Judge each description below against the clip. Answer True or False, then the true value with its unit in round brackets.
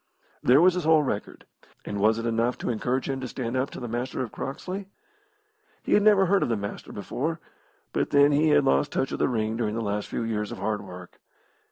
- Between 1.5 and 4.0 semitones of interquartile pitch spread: False (5.1 semitones)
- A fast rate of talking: True (230 wpm)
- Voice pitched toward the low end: True (120 Hz)